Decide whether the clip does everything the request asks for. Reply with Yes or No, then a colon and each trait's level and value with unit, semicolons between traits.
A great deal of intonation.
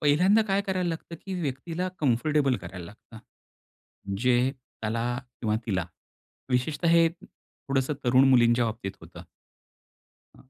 Yes: wide, 5.8 semitones